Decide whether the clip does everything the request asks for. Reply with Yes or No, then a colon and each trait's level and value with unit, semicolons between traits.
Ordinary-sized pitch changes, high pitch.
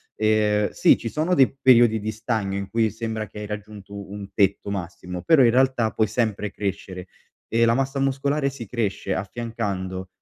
No: average, 3.2 semitones; low, 110 Hz